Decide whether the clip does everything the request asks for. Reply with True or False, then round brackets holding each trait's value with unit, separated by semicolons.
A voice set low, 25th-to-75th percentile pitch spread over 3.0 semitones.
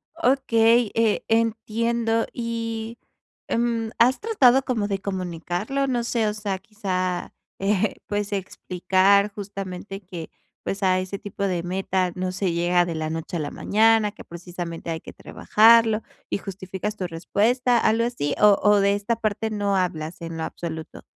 False (200 Hz; 3.7 semitones)